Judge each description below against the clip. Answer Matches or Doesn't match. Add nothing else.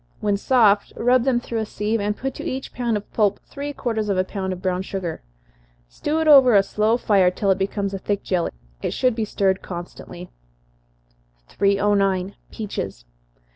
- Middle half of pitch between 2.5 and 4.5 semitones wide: Matches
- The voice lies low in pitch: Doesn't match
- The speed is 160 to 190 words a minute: Matches